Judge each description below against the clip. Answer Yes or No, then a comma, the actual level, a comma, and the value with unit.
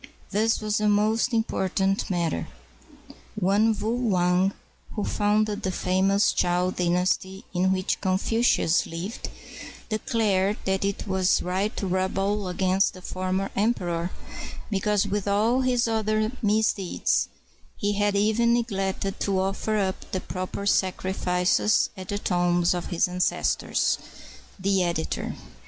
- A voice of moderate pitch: No, high, 195 Hz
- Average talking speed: No, slow, 125 wpm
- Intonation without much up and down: Yes, narrow, 2.3 semitones